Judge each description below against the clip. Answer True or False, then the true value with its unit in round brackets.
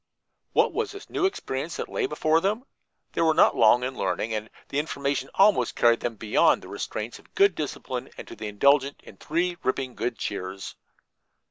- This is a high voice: False (140 Hz)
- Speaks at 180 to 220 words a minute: True (190 wpm)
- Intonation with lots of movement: True (6.4 semitones)